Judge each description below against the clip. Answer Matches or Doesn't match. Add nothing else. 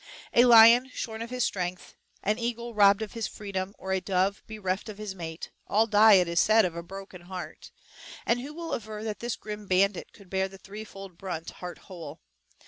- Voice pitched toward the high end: Matches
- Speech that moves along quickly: Matches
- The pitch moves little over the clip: Doesn't match